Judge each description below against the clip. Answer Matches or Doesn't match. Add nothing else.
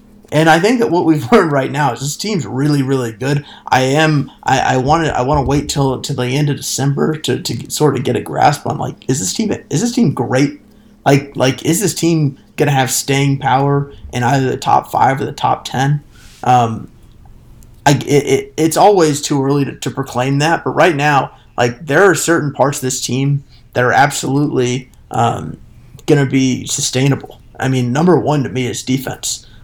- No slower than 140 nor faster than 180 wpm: Doesn't match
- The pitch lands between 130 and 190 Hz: Matches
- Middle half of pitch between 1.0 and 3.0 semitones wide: Matches